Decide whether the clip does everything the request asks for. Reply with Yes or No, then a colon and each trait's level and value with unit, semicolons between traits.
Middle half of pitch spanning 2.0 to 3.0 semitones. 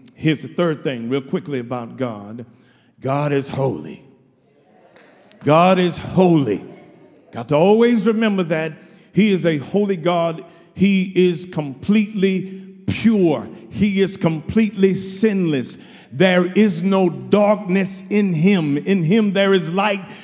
No: average, 4.2 semitones